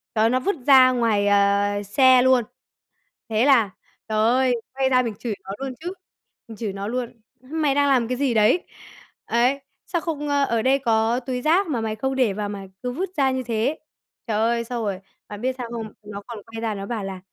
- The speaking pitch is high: Yes, high, 240 Hz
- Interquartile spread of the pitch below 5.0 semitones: Yes, average, 3.5 semitones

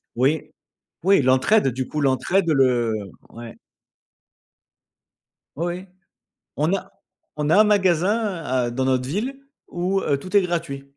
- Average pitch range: No, wide, 6.4 semitones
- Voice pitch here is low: No, medium, 155 Hz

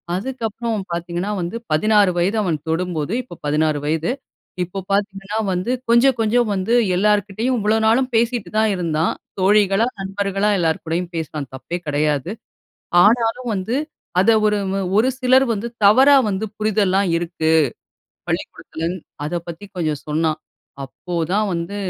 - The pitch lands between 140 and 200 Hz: Yes, high, 195 Hz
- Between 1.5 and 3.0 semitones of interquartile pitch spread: No, average, 4.4 semitones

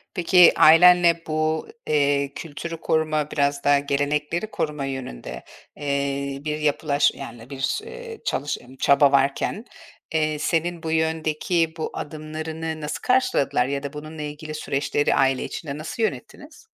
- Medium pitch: Yes, medium, 150 Hz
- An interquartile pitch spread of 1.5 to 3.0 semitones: Yes, narrow, 2.4 semitones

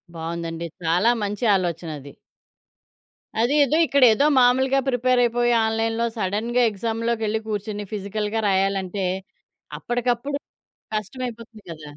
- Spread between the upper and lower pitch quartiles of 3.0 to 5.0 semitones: Yes, average, 3.9 semitones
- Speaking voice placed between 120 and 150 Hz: No, high, 220 Hz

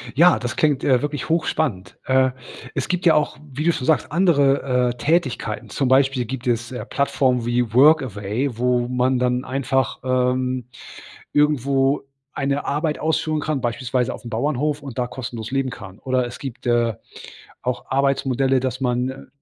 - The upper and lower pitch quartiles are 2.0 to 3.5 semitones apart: Yes, narrow, 2.4 semitones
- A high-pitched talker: No, low, 130 Hz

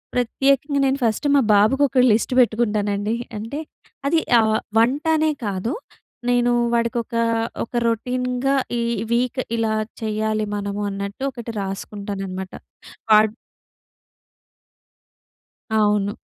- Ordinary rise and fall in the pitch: Yes, average, 3.3 semitones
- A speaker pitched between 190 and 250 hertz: Yes, high, 225 Hz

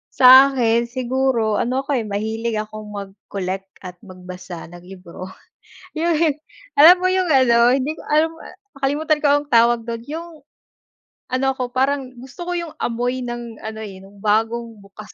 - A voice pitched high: Yes, high, 240 Hz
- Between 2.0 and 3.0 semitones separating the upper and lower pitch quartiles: No, average, 4.3 semitones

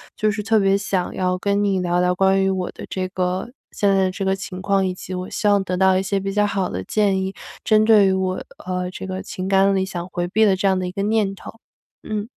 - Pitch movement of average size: No, narrow, 1.5 semitones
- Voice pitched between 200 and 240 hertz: No, high, 190 Hz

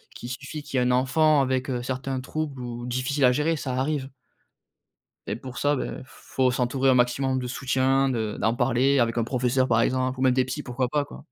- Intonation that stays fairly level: Yes, narrow, 1.5 semitones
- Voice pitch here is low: Yes, low, 130 Hz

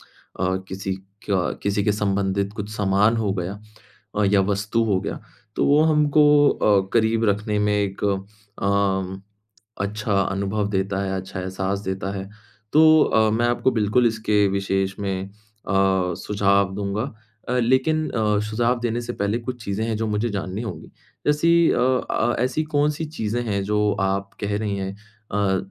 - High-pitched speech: No, low, 105 Hz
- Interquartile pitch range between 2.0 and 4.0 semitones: Yes, average, 2.9 semitones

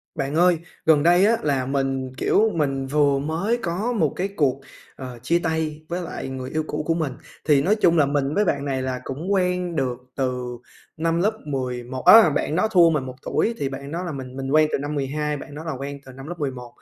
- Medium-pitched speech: Yes, medium, 145 Hz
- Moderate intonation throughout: Yes, average, 4.0 semitones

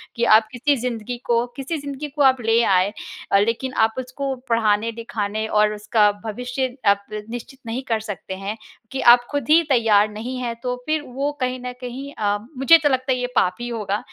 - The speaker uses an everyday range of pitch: Yes, average, 3.5 semitones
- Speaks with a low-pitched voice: No, high, 235 Hz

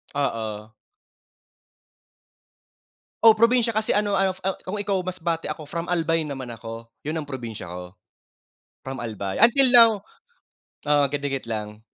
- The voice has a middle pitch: Yes, medium, 150 Hz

